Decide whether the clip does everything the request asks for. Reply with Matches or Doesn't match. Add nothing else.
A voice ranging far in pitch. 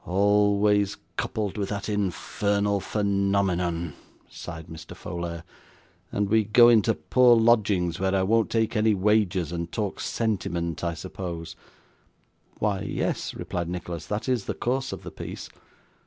Doesn't match